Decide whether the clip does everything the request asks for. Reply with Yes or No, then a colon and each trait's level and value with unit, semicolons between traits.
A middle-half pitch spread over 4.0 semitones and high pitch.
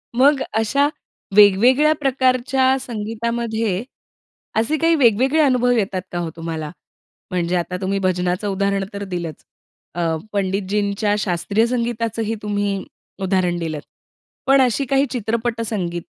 Yes: average, 4.7 semitones; high, 210 Hz